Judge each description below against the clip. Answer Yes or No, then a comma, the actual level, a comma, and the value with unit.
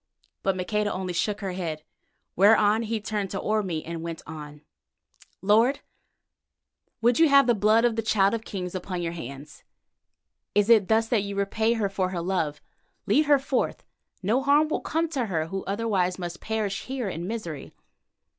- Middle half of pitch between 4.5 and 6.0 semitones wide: No, average, 4.0 semitones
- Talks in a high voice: Yes, high, 200 Hz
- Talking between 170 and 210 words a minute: Yes, average, 175 wpm